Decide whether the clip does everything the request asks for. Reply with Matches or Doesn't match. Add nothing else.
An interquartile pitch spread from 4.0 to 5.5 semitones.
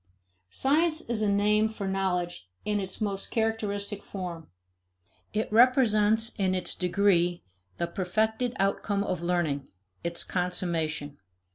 Doesn't match